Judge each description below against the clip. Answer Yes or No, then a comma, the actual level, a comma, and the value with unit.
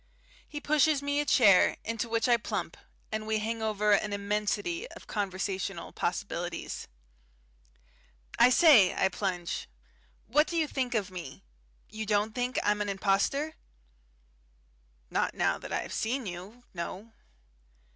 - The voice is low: No, high, 215 Hz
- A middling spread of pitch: Yes, average, 4.2 semitones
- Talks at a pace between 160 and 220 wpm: No, average, 140 wpm